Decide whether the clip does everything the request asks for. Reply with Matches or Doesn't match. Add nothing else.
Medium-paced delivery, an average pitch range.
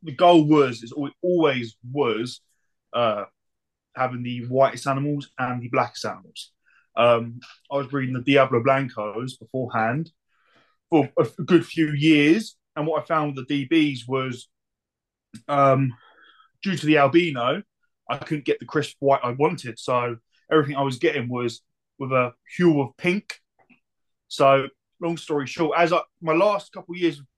Matches